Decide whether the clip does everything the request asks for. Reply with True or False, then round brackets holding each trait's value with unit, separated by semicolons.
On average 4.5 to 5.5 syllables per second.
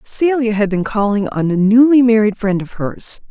True (4.8 syllables/s)